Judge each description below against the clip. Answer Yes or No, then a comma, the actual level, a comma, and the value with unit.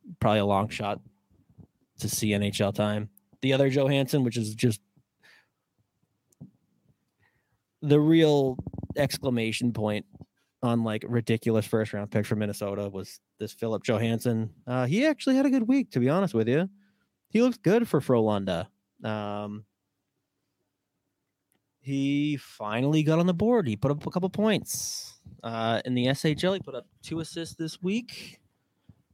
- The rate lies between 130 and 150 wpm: Yes, average, 145 wpm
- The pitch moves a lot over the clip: Yes, wide, 6.8 semitones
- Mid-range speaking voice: No, low, 125 Hz